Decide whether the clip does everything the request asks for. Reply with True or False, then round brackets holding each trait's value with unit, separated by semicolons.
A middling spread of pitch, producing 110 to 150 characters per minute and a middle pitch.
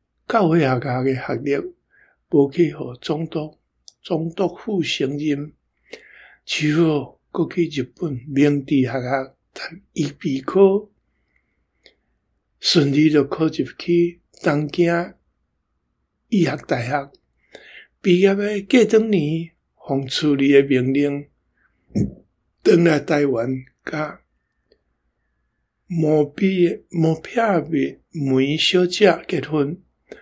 True (4.1 semitones; 140 characters per minute; 150 Hz)